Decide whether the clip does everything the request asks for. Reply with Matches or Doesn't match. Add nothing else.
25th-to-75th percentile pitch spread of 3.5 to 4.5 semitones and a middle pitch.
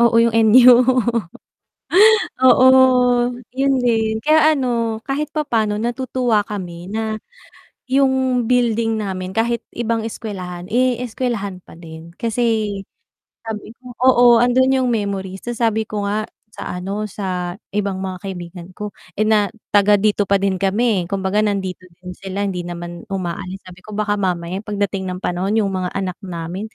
Doesn't match